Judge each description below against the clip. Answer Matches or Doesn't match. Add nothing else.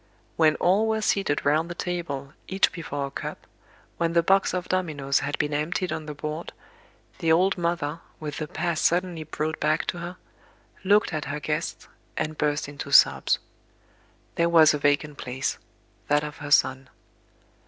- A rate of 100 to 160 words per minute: Doesn't match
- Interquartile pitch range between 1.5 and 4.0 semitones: Matches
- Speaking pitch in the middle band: Matches